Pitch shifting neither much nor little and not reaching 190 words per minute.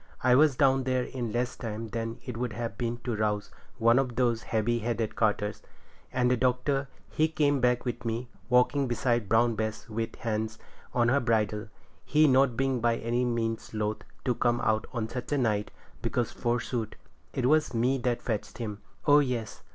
No: narrow, 2.1 semitones; average, 180 wpm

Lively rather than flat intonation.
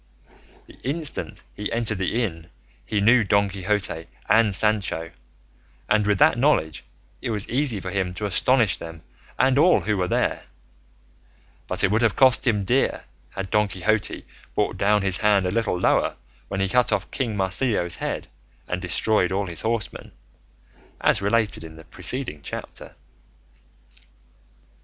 No: average, 3.7 semitones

